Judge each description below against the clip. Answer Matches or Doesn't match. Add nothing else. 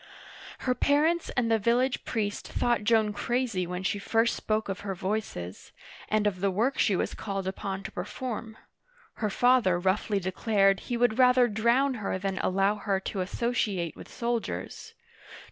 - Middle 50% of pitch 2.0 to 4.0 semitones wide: Matches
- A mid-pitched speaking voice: Doesn't match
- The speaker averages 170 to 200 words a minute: Doesn't match